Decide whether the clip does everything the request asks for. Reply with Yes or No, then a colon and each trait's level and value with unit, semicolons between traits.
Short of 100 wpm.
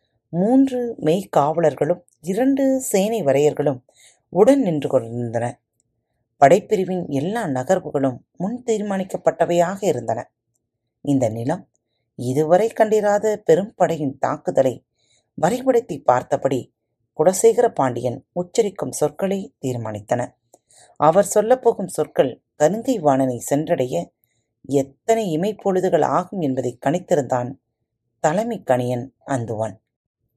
Yes: average, 85 wpm